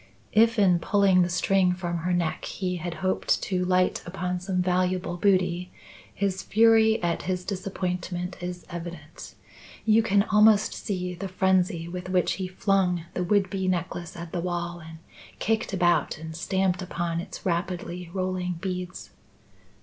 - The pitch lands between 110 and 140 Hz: No, medium, 180 Hz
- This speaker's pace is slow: No, average, 155 wpm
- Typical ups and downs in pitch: No, narrow, 1.5 semitones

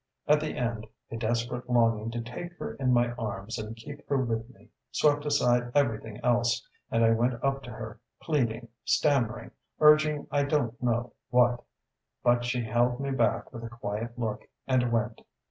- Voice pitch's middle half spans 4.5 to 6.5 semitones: No, average, 2.7 semitones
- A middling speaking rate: Yes, average, 175 wpm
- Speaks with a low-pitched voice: Yes, low, 120 Hz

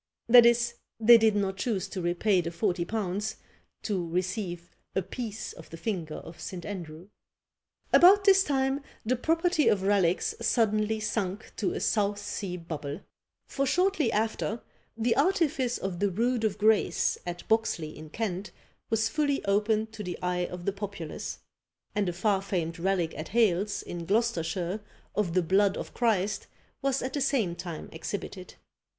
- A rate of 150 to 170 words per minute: Yes, average, 160 wpm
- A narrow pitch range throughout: No, average, 4.2 semitones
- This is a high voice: Yes, high, 205 Hz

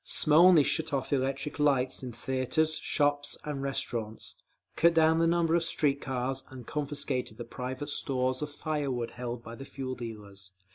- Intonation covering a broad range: No, average, 3.0 semitones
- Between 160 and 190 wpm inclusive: Yes, average, 175 wpm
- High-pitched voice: No, low, 135 Hz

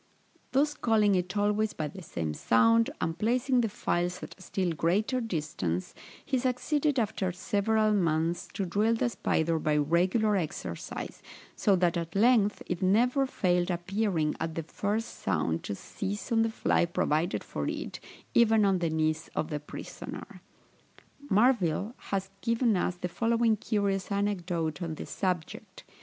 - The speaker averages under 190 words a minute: Yes, average, 155 wpm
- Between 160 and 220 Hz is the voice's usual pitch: Yes, high, 190 Hz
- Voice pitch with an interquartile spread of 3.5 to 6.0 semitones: Yes, average, 4.9 semitones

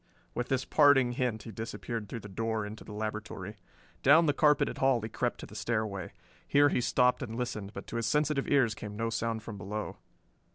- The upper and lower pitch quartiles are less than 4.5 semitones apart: Yes, average, 3.2 semitones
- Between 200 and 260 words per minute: Yes, fast, 205 wpm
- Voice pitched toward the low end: Yes, low, 115 Hz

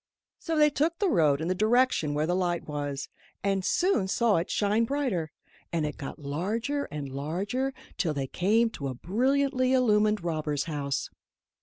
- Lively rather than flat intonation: Yes, wide, 8.6 semitones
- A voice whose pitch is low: No, high, 190 Hz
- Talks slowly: No, average, 170 wpm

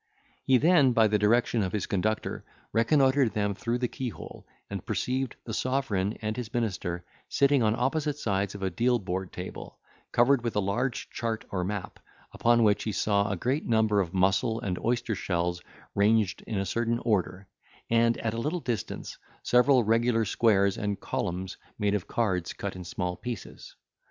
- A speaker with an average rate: Yes, average, 175 wpm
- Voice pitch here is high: No, low, 110 Hz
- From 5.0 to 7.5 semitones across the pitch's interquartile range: No, average, 3.6 semitones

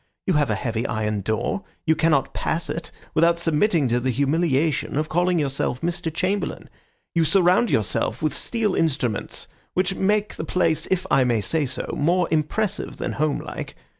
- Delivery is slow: No, average, 165 wpm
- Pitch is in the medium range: Yes, medium, 160 Hz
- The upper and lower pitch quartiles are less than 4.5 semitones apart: No, average, 5.0 semitones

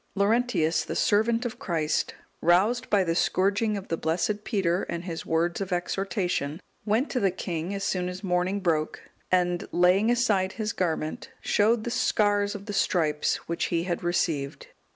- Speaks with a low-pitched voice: No, medium, 185 Hz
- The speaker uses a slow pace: No, average, 170 wpm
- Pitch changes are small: No, average, 3.4 semitones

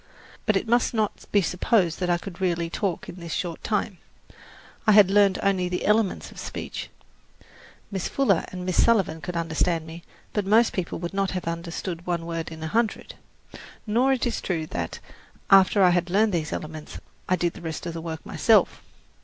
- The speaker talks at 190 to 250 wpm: Yes, average, 195 wpm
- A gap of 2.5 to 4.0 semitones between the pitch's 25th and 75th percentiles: Yes, average, 3.2 semitones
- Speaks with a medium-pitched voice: Yes, medium, 180 Hz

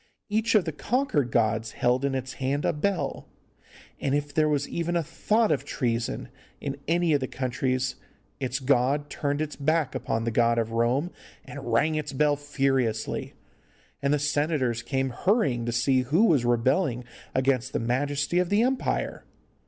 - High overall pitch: No, medium, 140 Hz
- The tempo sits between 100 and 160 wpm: No, average, 170 wpm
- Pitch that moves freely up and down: No, average, 3.8 semitones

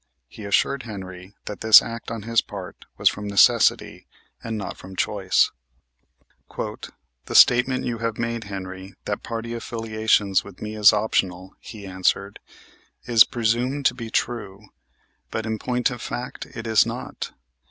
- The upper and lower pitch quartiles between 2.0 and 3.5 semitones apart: Yes, average, 2.8 semitones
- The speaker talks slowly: No, average, 150 wpm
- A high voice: No, low, 110 Hz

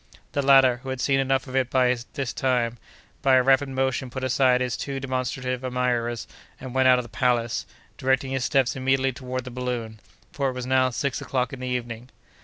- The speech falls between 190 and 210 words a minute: Yes, fast, 205 wpm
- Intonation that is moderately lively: No, narrow, 1.1 semitones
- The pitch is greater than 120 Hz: Yes, low, 130 Hz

